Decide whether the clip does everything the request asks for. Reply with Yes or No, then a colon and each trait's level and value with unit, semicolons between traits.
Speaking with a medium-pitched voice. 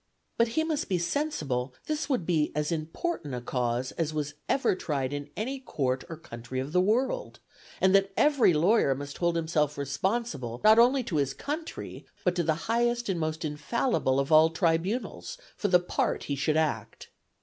Yes: medium, 165 Hz